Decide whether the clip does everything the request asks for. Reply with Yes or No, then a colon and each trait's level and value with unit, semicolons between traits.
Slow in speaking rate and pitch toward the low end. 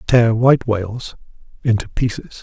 Yes: slow, 125 wpm; low, 115 Hz